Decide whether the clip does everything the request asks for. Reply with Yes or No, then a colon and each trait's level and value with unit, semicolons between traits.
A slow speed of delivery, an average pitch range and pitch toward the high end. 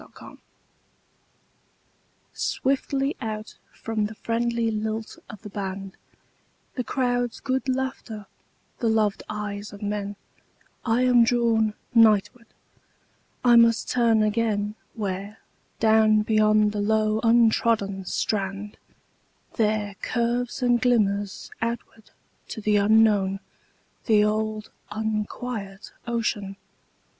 No: slow, 90 wpm; narrow, 2.0 semitones; high, 220 Hz